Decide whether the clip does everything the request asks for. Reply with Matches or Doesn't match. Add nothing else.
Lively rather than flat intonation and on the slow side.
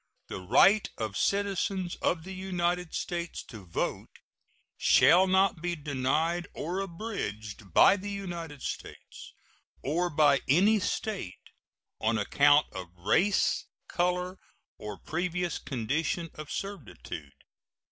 Matches